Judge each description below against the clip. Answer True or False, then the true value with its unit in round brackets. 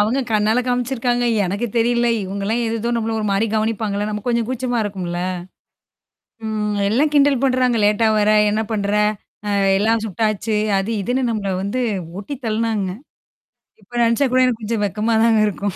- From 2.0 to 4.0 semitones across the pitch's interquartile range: True (2.6 semitones)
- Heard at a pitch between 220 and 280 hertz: True (225 Hz)